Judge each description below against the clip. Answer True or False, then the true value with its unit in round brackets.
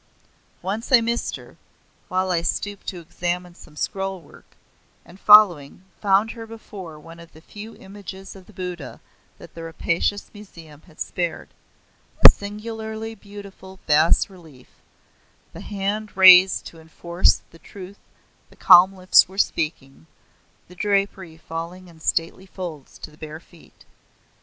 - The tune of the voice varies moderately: True (3.4 semitones)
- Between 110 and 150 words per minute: True (140 wpm)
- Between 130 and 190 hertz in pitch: True (185 Hz)